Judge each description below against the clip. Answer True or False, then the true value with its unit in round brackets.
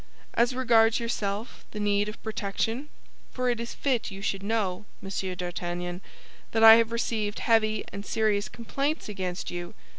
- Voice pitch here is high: True (215 Hz)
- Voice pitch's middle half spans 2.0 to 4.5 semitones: True (2.9 semitones)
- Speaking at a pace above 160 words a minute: False (155 wpm)